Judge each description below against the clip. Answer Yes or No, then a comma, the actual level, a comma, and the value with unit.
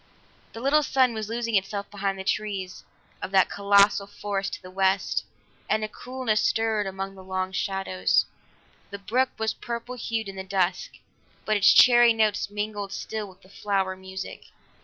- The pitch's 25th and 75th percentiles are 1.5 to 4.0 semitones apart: Yes, narrow, 2.5 semitones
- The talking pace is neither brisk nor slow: Yes, average, 165 wpm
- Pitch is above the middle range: Yes, high, 200 Hz